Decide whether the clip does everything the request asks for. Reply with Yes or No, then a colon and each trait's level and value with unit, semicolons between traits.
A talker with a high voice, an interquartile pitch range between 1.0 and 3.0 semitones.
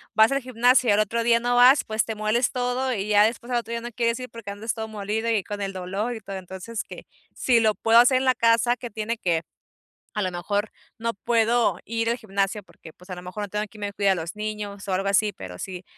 Yes: high, 220 Hz; narrow, 2.6 semitones